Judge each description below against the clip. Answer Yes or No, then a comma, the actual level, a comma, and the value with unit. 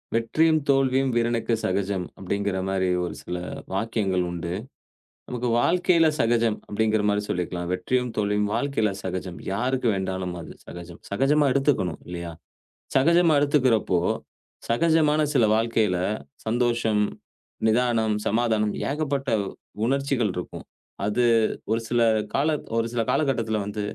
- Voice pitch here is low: Yes, low, 115 Hz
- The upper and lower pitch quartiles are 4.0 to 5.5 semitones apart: Yes, average, 4.9 semitones